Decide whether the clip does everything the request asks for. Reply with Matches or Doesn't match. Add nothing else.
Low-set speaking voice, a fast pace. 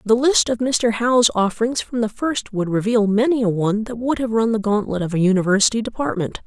Doesn't match